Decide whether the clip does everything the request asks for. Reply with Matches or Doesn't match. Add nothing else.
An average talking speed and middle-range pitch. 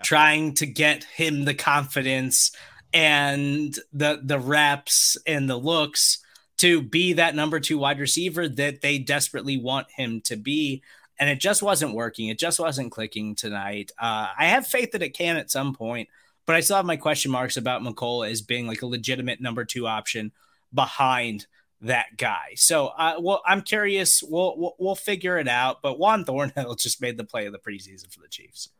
Matches